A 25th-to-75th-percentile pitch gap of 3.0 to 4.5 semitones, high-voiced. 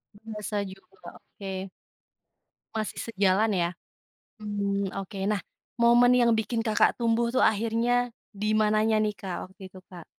No: narrow, 2.6 semitones; high, 215 Hz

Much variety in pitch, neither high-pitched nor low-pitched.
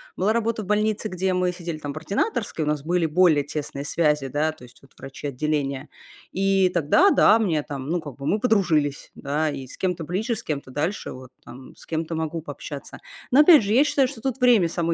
Yes: wide, 6.1 semitones; medium, 165 Hz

